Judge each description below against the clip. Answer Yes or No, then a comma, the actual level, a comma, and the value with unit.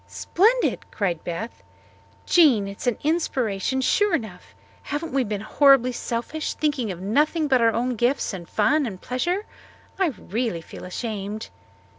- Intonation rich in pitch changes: Yes, wide, 6.1 semitones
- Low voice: No, high, 245 Hz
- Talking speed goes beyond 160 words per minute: No, average, 150 wpm